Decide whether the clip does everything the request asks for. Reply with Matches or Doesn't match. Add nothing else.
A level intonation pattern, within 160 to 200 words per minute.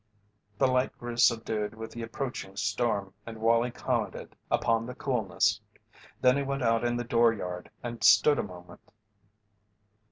Doesn't match